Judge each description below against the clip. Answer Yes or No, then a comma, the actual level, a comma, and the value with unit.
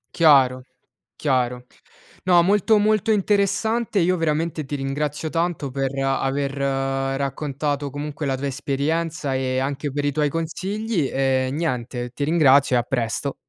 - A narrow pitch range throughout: No, average, 3.5 semitones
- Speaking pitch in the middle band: Yes, medium, 145 Hz